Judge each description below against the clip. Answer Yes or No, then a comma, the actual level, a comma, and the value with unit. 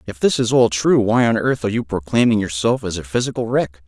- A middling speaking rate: No, fast, 250 wpm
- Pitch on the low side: Yes, low, 110 Hz